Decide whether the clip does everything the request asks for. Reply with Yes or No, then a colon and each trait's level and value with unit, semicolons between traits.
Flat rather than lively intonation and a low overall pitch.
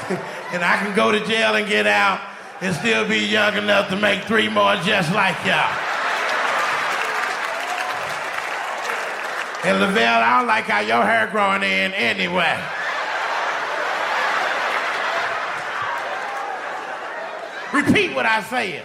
No: narrow, 1.7 semitones; high, 210 Hz